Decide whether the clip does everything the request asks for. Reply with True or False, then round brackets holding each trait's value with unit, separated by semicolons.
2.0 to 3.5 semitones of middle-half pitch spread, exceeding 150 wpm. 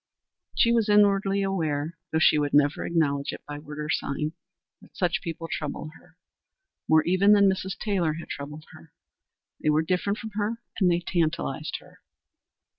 False (4.5 semitones; 170 wpm)